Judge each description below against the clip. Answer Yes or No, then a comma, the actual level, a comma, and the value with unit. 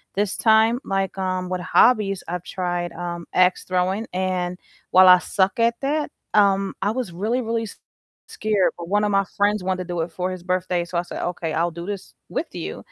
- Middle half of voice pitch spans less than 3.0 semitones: Yes, narrow, 2.6 semitones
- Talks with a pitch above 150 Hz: Yes, medium, 185 Hz